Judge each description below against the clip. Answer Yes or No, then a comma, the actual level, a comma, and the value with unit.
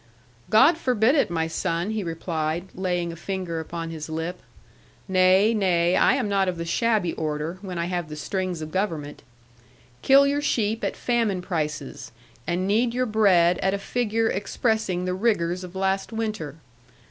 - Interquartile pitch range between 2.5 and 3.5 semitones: No, average, 4.4 semitones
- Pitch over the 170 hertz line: Yes, medium, 185 Hz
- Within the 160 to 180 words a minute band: Yes, average, 170 wpm